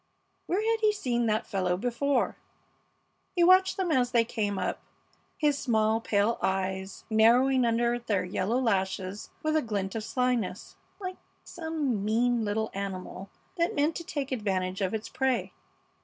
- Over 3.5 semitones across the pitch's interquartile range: Yes, wide, 5.5 semitones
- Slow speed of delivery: No, average, 155 wpm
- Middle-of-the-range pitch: No, high, 230 Hz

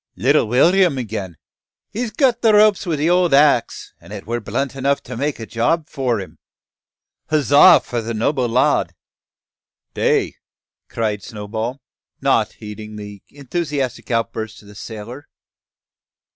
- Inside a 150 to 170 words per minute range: No, average, 140 wpm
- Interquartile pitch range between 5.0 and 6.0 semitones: Yes, wide, 5.4 semitones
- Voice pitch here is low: Yes, low, 125 Hz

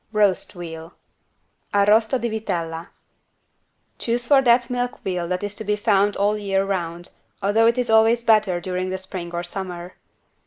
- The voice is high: Yes, high, 200 Hz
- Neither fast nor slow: Yes, average, 170 wpm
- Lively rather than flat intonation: No, average, 3.6 semitones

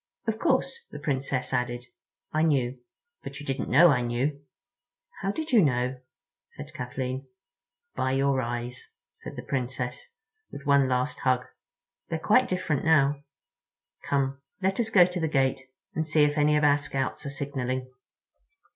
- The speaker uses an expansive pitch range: No, average, 3.3 semitones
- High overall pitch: No, medium, 140 Hz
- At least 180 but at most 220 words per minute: No, average, 155 wpm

